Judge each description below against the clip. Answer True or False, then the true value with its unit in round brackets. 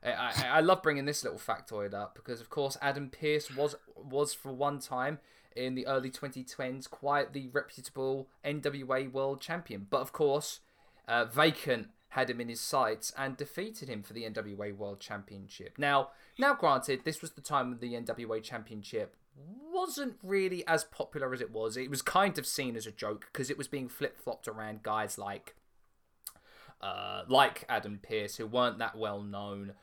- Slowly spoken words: False (180 wpm)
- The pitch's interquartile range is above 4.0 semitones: True (4.6 semitones)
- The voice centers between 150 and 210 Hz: False (135 Hz)